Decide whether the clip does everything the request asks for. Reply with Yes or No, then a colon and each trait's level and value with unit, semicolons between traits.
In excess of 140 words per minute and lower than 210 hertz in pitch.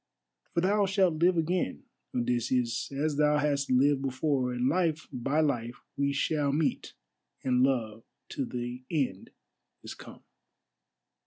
No: slow, 135 wpm; medium, 140 Hz